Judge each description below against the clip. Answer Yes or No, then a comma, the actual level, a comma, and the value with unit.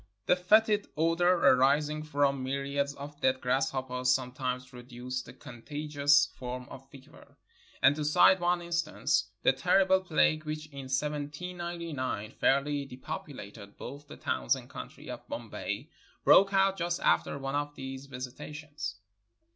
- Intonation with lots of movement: No, average, 3.2 semitones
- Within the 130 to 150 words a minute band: Yes, average, 140 wpm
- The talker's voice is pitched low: No, medium, 145 Hz